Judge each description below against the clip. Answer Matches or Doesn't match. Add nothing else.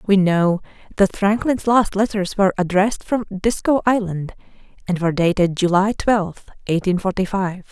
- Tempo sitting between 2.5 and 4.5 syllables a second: Doesn't match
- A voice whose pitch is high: Matches